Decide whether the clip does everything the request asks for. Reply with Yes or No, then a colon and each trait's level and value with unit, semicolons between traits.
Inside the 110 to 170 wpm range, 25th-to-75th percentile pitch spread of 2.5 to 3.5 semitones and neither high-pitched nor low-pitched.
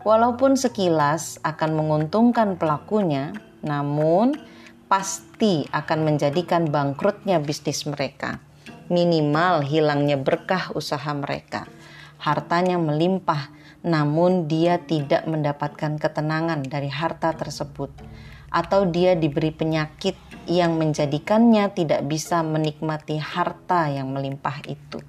No: average, 95 wpm; average, 2.9 semitones; medium, 160 Hz